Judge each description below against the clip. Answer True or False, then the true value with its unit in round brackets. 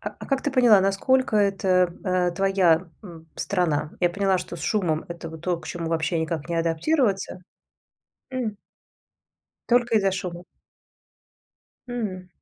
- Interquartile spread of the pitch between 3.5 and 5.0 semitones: True (3.9 semitones)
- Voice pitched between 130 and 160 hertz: False (185 Hz)